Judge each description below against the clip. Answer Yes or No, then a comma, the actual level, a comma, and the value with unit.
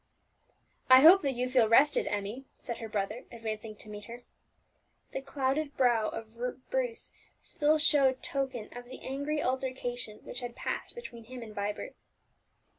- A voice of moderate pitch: No, very high, 250 Hz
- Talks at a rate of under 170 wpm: Yes, average, 155 wpm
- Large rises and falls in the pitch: No, average, 3.4 semitones